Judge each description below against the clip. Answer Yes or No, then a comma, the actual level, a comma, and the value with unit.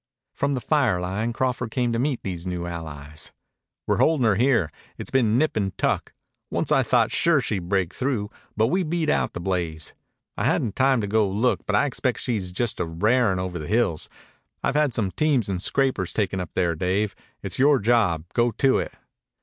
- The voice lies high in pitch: No, low, 110 Hz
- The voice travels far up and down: Yes, wide, 5.9 semitones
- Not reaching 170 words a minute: No, average, 200 wpm